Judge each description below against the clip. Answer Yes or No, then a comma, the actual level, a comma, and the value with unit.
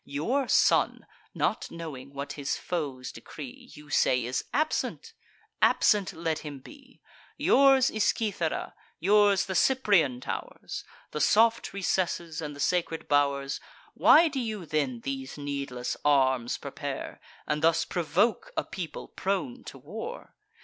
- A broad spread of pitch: Yes, wide, 7.4 semitones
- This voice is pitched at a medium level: Yes, medium, 165 Hz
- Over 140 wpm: No, slow, 135 wpm